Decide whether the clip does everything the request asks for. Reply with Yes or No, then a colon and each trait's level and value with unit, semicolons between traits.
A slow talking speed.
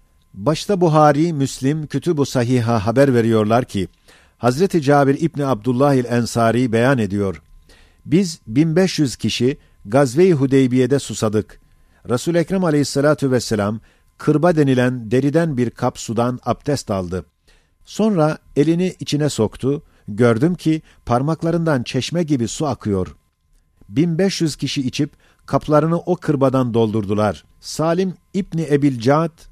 No: average, 110 wpm